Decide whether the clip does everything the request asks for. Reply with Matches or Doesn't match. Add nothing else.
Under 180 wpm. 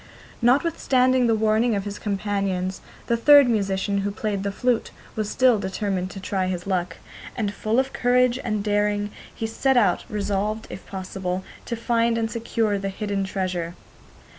Matches